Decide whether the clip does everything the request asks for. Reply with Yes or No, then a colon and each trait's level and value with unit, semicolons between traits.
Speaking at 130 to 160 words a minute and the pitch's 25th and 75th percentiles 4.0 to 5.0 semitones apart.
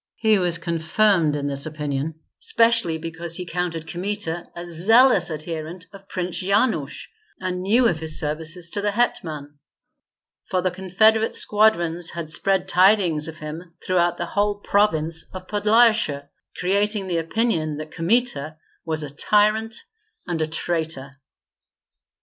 Yes: average, 140 wpm; average, 4.4 semitones